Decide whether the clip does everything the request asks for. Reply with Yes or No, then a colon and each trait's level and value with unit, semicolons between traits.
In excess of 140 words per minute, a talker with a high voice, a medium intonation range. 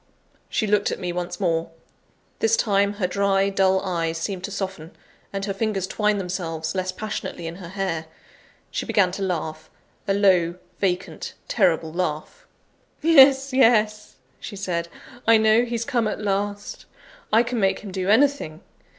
Yes: average, 160 wpm; high, 195 Hz; average, 3.1 semitones